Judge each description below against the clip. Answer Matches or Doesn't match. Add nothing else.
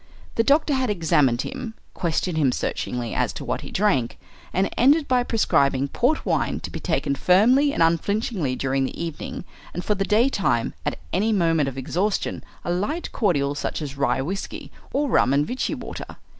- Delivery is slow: Doesn't match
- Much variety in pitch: Matches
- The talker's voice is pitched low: Doesn't match